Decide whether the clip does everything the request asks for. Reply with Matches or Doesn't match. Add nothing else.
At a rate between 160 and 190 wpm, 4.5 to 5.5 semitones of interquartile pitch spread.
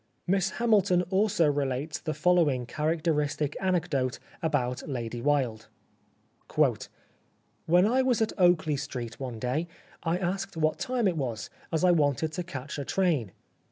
Doesn't match